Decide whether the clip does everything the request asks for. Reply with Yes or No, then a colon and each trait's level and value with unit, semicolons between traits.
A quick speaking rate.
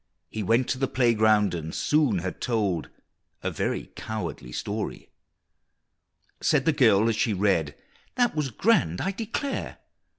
No: average, 140 wpm